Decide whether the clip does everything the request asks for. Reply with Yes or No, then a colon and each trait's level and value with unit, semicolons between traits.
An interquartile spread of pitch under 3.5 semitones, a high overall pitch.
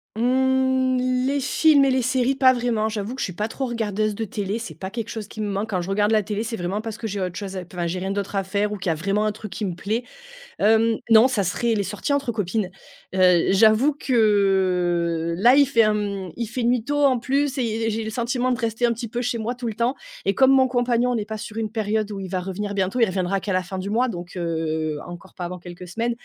No: average, 3.9 semitones; high, 215 Hz